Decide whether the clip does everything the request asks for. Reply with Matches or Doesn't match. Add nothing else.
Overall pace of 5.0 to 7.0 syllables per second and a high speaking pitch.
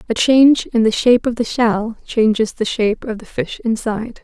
Matches